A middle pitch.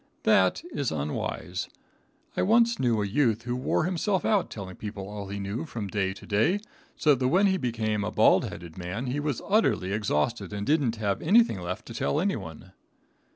No: low, 115 Hz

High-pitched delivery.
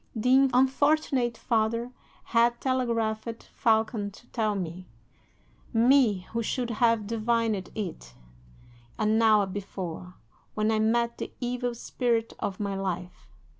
Yes: high, 225 Hz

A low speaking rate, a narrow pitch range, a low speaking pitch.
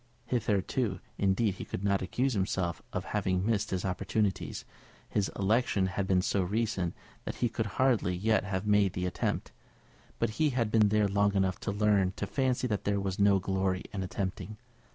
No: average, 180 wpm; narrow, 2.3 semitones; low, 100 Hz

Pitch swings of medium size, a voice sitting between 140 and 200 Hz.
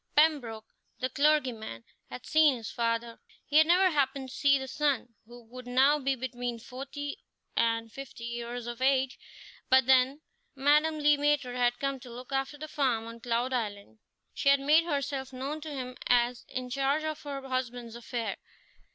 No: average, 3.1 semitones; very high, 260 Hz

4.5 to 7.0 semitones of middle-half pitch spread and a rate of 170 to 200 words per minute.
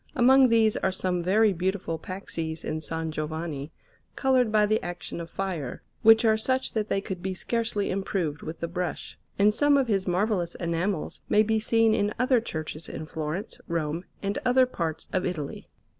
Yes: average, 4.8 semitones; average, 180 wpm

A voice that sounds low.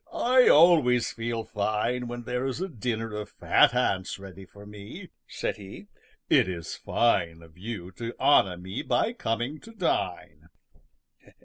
Yes: low, 115 Hz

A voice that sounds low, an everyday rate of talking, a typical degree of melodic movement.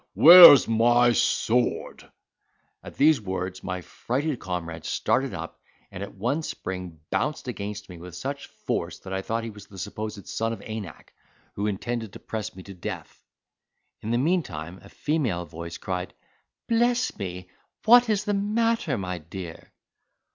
No: low, 105 Hz; average, 155 wpm; wide, 7.2 semitones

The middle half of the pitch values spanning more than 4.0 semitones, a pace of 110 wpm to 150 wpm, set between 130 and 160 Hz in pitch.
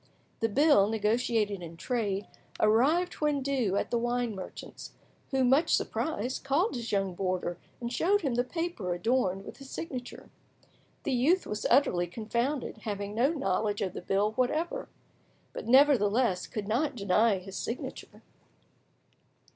No: average, 5.2 semitones; average, 145 wpm; high, 235 Hz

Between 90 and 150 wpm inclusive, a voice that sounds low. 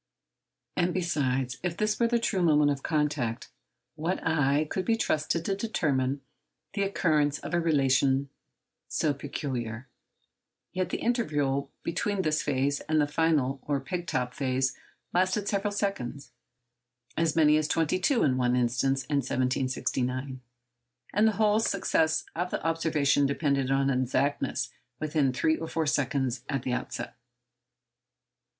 No: average, 140 wpm; medium, 145 Hz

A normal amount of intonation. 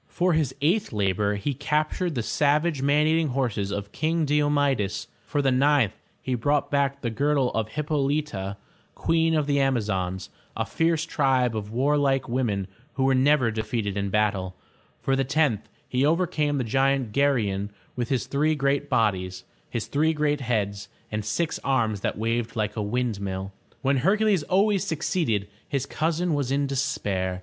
No: wide, 5.7 semitones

